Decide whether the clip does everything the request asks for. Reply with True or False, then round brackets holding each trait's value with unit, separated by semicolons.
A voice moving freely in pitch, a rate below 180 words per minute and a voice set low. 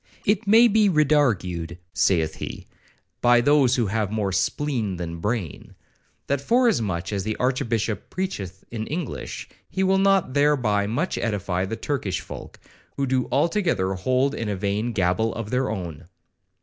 True (7.0 semitones; 150 wpm; 115 Hz)